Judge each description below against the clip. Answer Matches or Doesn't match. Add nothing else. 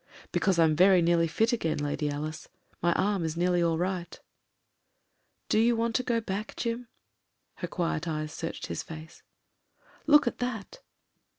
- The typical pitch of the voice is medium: Matches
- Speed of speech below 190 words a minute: Matches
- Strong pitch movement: Matches